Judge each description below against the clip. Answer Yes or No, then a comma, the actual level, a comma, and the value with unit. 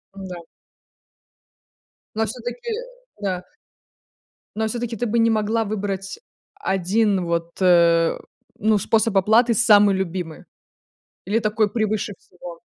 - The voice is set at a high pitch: Yes, high, 205 Hz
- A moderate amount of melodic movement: Yes, average, 3.4 semitones